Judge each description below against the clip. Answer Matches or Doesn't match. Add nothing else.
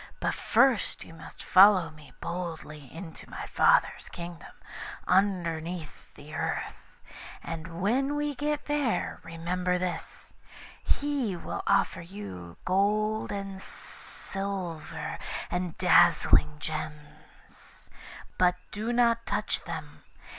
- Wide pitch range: Doesn't match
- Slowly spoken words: Matches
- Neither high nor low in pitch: Matches